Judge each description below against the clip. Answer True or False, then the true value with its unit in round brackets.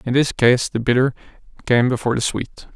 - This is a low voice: True (125 Hz)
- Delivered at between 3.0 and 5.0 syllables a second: False (5.6 syllables/s)